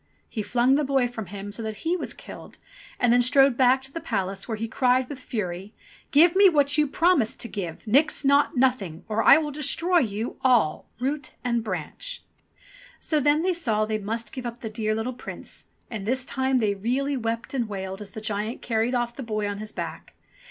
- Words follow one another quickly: Yes, fast, 210 wpm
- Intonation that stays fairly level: No, average, 4.4 semitones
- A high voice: Yes, high, 240 Hz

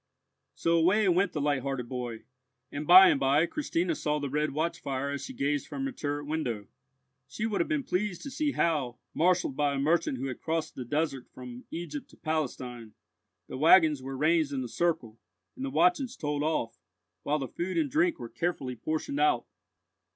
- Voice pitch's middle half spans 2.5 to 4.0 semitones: No, average, 4.8 semitones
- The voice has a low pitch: No, medium, 150 Hz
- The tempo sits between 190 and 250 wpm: Yes, average, 195 wpm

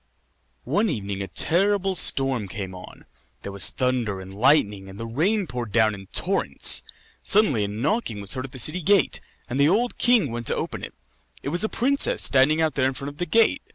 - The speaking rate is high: Yes, fast, 210 wpm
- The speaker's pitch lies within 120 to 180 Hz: Yes, low, 135 Hz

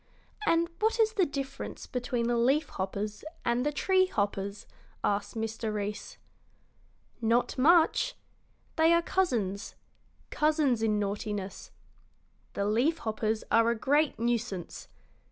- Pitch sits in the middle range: No, high, 235 Hz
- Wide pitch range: Yes, wide, 6.6 semitones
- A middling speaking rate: No, slow, 120 wpm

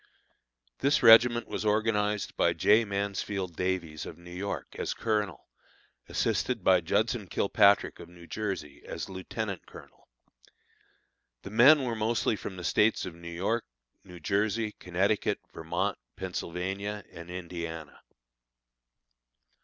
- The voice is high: No, low, 100 Hz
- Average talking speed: No, slow, 120 wpm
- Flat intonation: No, average, 3.5 semitones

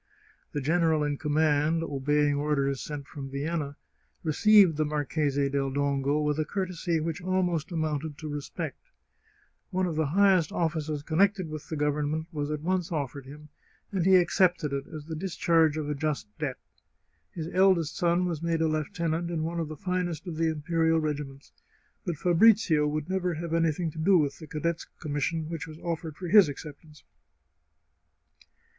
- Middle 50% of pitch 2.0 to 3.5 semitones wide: Yes, narrow, 2.5 semitones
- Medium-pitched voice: Yes, medium, 155 Hz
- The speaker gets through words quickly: No, average, 175 wpm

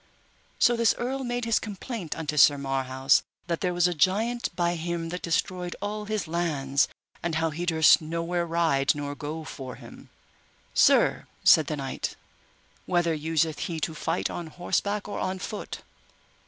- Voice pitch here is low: No, medium, 170 Hz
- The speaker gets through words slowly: No, average, 165 wpm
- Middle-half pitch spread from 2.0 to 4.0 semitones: Yes, average, 3.4 semitones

